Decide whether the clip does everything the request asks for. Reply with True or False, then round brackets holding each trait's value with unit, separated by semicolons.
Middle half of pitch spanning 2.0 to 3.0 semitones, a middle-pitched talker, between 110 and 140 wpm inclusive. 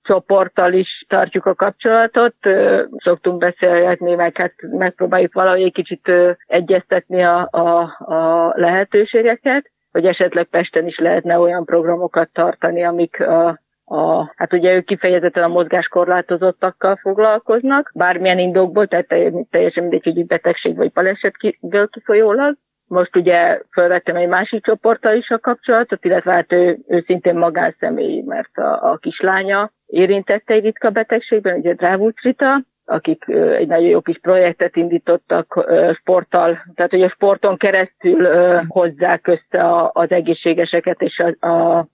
True (2.6 semitones; 180 Hz; 130 wpm)